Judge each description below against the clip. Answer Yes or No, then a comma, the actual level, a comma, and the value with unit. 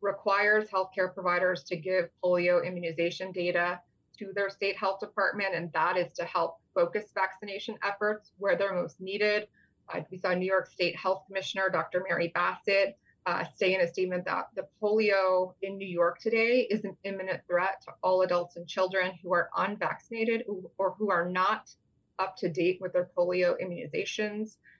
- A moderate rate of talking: Yes, average, 170 wpm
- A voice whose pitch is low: No, high, 190 Hz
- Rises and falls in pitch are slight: Yes, narrow, 2.0 semitones